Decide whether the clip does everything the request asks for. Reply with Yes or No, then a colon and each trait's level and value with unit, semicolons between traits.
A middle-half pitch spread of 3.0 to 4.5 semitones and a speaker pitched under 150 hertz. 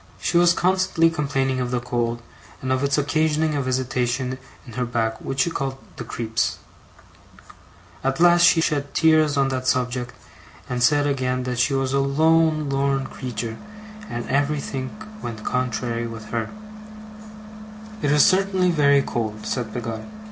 Yes: average, 3.3 semitones; low, 135 Hz